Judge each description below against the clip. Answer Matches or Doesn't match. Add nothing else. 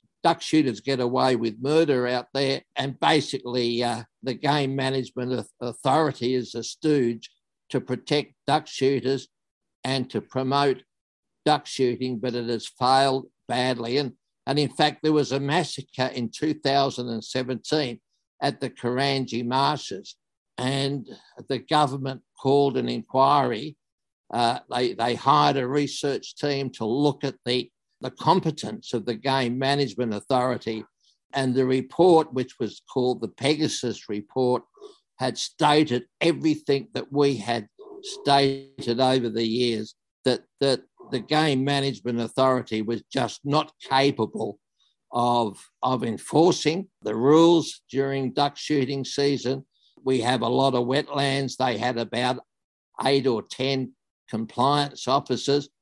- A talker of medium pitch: Doesn't match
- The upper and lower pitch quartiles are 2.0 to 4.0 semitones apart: Matches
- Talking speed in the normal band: Doesn't match